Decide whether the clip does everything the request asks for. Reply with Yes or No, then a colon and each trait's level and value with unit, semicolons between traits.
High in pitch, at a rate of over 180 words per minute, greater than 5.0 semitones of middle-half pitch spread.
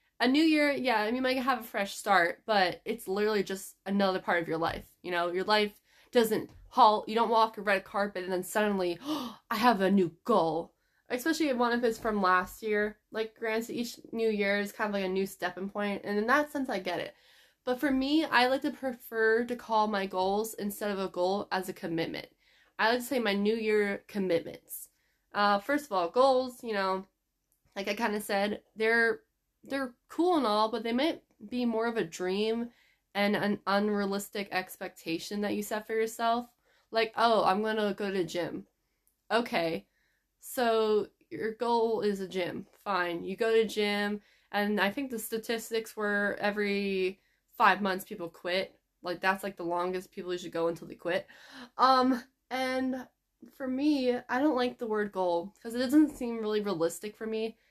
No: high, 215 Hz; average, 200 wpm; average, 3.6 semitones